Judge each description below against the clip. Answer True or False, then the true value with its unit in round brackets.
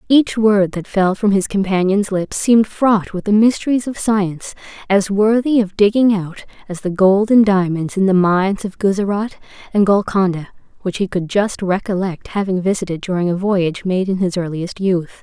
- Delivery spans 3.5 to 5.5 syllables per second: True (5.0 syllables/s)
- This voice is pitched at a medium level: False (195 Hz)